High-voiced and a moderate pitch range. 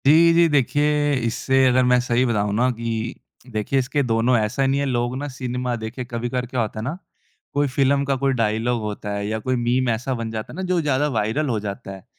No: low, 125 Hz; average, 3.2 semitones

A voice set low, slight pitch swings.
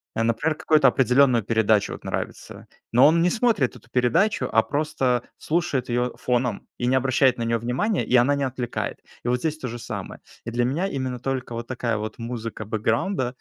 No: low, 125 Hz; average, 3.2 semitones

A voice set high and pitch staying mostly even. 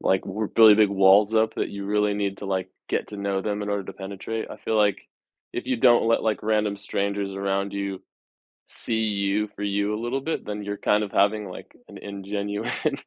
No: low, 100 Hz; narrow, 1.3 semitones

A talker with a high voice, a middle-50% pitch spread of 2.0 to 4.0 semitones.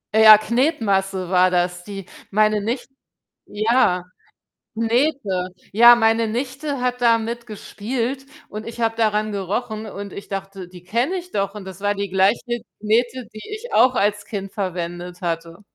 Yes: high, 215 Hz; average, 3.6 semitones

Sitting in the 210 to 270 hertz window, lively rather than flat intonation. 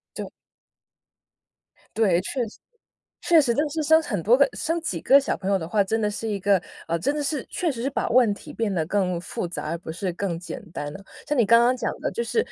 Yes: high, 220 Hz; wide, 6.9 semitones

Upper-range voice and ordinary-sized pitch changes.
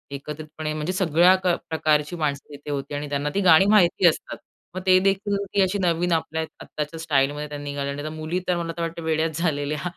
No: medium, 160 Hz; average, 3.1 semitones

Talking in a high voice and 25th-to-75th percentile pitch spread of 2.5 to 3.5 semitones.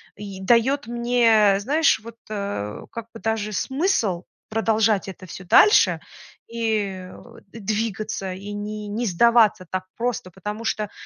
Yes: high, 215 Hz; average, 2.8 semitones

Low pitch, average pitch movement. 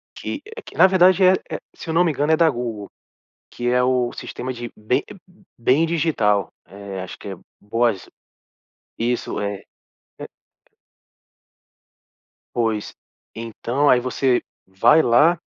No: low, 120 Hz; wide, 6.2 semitones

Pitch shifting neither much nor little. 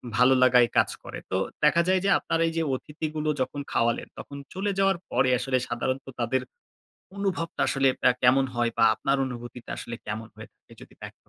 Yes: average, 4.5 semitones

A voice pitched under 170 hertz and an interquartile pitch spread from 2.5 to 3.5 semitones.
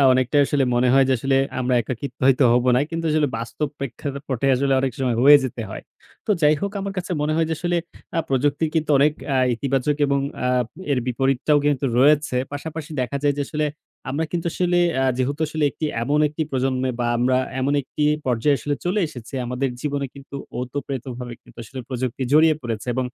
Yes: medium, 140 Hz; average, 2.8 semitones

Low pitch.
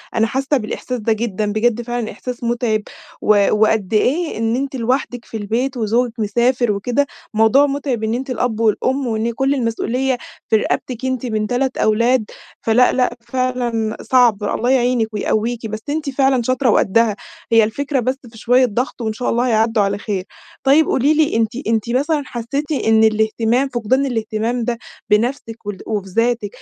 No: high, 235 Hz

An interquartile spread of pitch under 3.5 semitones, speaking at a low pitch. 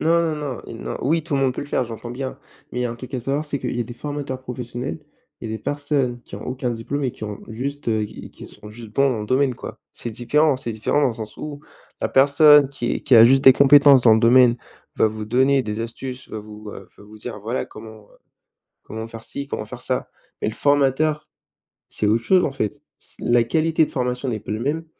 No: average, 3.8 semitones; low, 125 Hz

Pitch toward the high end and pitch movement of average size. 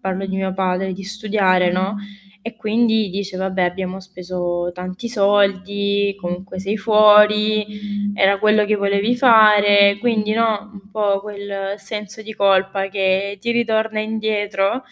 No: high, 200 Hz; narrow, 1.8 semitones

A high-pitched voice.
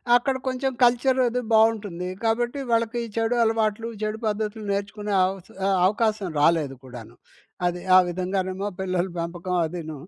Yes: high, 210 Hz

